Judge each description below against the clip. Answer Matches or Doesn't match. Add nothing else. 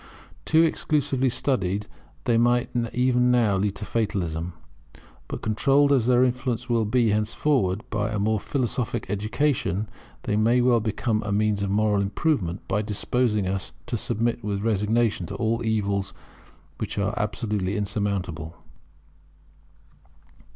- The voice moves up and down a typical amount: Matches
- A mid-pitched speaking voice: Doesn't match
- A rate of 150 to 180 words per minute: Doesn't match